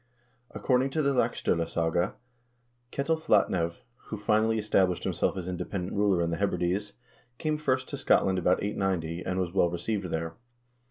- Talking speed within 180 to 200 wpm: No, average, 155 wpm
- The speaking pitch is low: Yes, very low, 95 Hz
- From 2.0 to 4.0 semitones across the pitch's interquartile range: No, average, 4.5 semitones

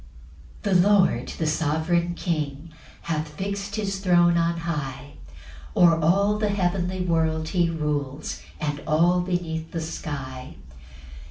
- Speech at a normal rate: No, slow, 125 wpm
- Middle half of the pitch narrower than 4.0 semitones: Yes, average, 2.9 semitones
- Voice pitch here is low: No, medium, 170 Hz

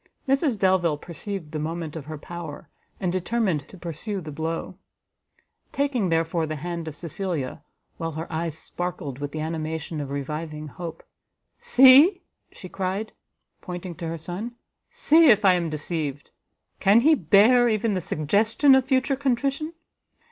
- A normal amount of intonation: No, wide, 5.7 semitones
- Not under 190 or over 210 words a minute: No, average, 150 wpm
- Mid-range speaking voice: Yes, medium, 175 Hz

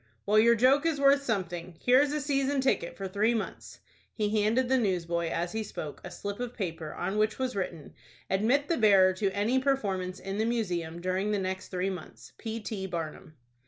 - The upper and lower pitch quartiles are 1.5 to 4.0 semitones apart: No, average, 5.0 semitones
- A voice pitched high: Yes, high, 205 Hz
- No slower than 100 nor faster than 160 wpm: No, average, 200 wpm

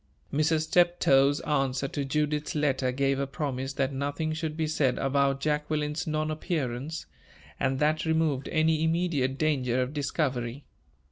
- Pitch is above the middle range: No, medium, 145 Hz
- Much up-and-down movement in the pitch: No, narrow, 2.5 semitones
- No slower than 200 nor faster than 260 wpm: No, average, 140 wpm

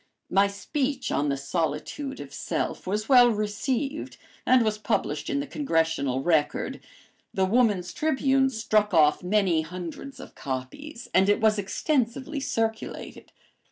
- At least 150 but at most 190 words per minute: No, slow, 135 wpm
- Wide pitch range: Yes, wide, 7.1 semitones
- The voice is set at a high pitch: Yes, high, 210 Hz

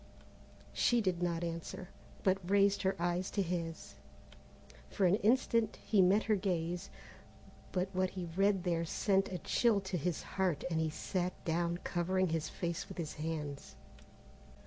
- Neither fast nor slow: Yes, average, 155 wpm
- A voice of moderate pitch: Yes, medium, 180 Hz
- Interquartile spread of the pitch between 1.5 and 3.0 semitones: Yes, narrow, 2.5 semitones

